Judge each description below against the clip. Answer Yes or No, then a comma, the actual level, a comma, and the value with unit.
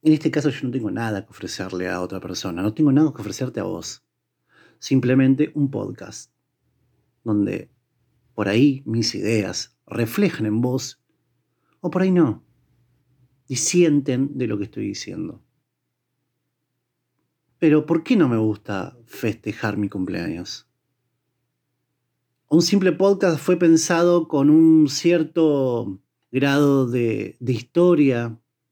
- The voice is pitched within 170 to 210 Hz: No, low, 130 Hz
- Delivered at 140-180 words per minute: No, average, 130 wpm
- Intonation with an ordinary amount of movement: No, wide, 6.2 semitones